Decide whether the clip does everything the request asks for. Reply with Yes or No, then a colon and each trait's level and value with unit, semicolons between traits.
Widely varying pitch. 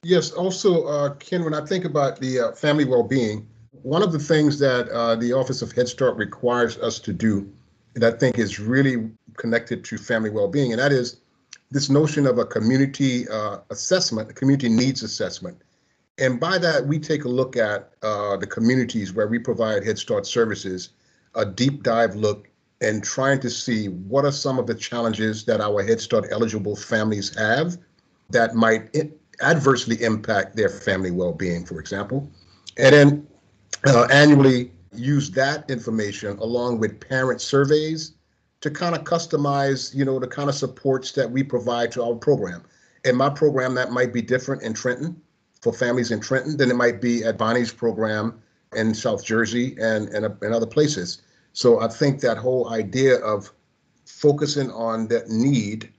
No: average, 3.9 semitones